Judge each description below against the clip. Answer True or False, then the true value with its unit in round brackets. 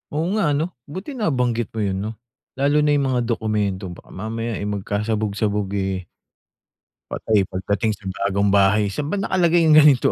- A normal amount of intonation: False (6.4 semitones)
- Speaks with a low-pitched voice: True (110 Hz)